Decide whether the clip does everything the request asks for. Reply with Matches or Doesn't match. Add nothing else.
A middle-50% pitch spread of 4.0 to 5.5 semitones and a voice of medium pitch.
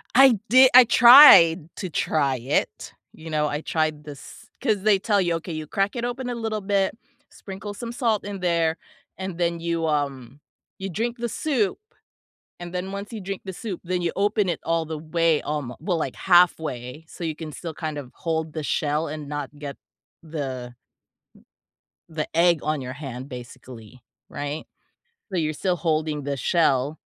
Matches